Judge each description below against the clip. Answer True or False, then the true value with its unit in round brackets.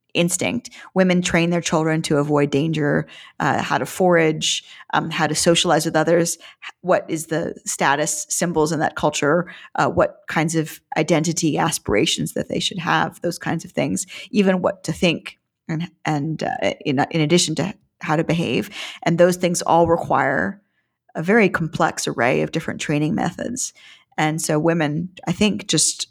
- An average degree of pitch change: False (1.9 semitones)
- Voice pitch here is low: False (165 Hz)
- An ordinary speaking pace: True (170 wpm)